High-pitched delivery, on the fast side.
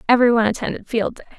No: high, 230 Hz; average, 175 wpm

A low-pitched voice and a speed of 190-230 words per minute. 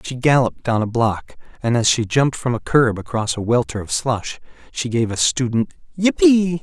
Yes: low, 120 Hz; average, 200 wpm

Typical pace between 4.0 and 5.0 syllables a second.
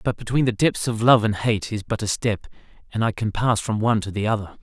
No: 5.9 syllables/s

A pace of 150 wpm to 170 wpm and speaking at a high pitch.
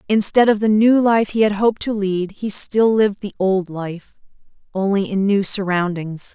No: average, 190 wpm; high, 200 Hz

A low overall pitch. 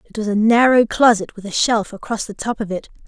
No: high, 220 Hz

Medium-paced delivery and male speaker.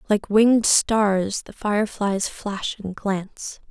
No: average, 145 wpm; female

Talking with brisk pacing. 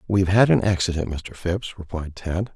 No: average, 190 wpm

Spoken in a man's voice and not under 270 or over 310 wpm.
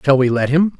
Yes: male; fast, 305 wpm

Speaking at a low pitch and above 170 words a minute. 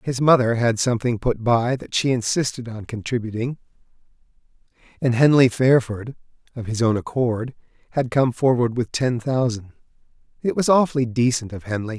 No: low, 120 Hz; average, 150 wpm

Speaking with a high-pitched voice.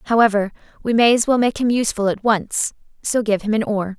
Yes: high, 220 Hz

